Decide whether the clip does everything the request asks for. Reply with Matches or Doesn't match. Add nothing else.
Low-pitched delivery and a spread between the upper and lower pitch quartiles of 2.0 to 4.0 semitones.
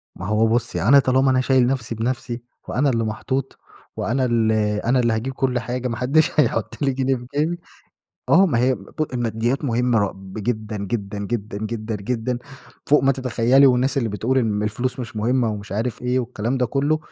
Matches